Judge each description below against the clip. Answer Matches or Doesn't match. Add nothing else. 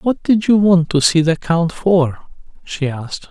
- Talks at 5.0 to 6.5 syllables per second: Doesn't match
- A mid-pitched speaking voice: Matches